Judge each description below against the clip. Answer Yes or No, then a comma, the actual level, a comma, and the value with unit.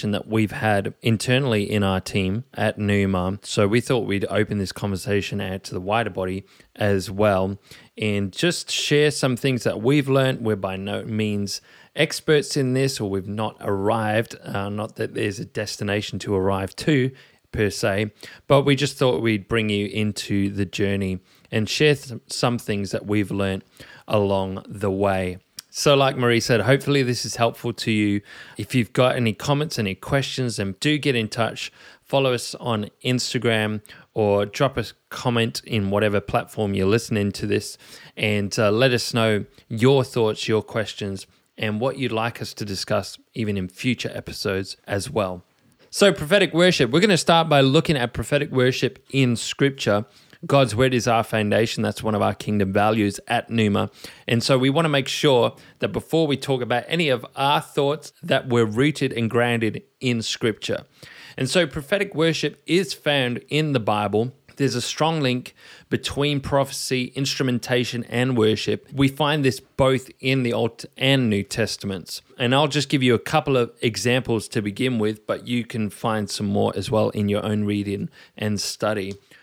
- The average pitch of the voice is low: Yes, low, 115 Hz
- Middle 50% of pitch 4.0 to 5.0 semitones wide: Yes, average, 4.5 semitones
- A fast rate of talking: No, average, 180 wpm